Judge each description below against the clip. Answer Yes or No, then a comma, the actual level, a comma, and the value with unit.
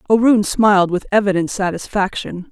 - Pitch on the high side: Yes, high, 200 Hz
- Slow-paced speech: Yes, slow, 120 wpm